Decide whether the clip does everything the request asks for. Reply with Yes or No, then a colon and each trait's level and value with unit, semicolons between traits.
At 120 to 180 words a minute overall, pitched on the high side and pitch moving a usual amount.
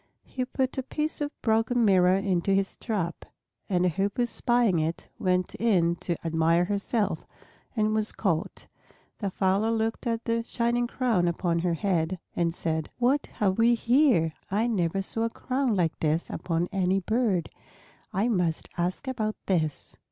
Yes: average, 160 wpm; high, 195 Hz; average, 4.9 semitones